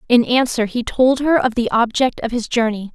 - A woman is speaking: Yes, female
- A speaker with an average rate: No, fast, 225 wpm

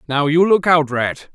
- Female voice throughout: No, male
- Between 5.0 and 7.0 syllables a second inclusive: No, 4.4 syllables/s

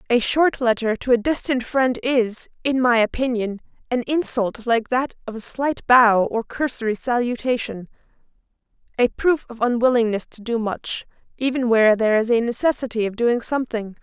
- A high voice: Yes, high, 240 Hz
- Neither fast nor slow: Yes, average, 160 wpm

